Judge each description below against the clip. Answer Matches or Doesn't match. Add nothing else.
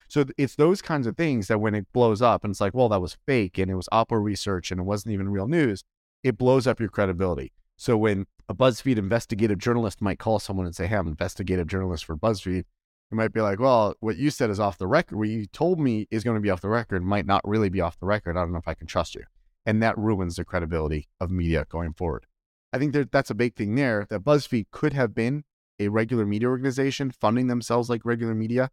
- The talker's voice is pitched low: Matches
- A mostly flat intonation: Doesn't match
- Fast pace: Matches